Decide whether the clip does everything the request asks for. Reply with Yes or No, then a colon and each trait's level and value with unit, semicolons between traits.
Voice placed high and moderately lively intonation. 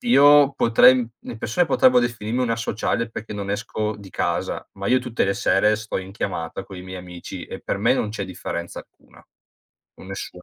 No: low, 105 Hz; average, 3.8 semitones